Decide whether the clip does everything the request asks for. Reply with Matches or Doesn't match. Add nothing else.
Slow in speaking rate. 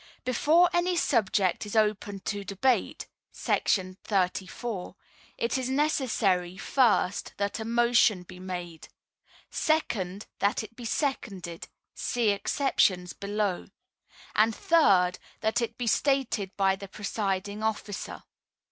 Matches